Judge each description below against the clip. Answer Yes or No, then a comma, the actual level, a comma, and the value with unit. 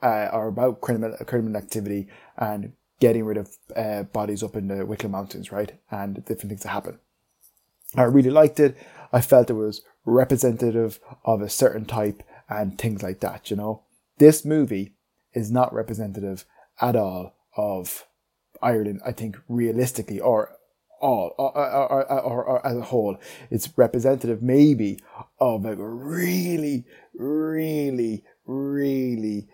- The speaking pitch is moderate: No, low, 115 Hz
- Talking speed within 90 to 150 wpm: Yes, average, 145 wpm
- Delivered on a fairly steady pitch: No, average, 3.9 semitones